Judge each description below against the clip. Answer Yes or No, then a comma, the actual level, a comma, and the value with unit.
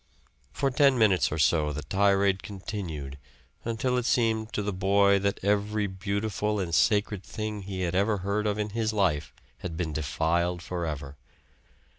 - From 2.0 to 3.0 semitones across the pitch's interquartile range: No, average, 3.4 semitones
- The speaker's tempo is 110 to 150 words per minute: No, average, 160 wpm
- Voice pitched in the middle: No, low, 100 Hz